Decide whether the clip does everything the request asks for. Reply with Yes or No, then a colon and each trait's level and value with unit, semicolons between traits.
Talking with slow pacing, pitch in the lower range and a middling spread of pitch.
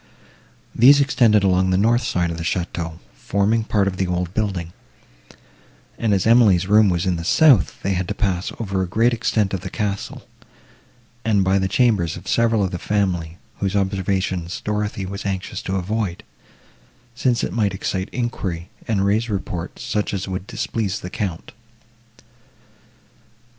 No: average, 165 wpm; low, 100 Hz; average, 3.0 semitones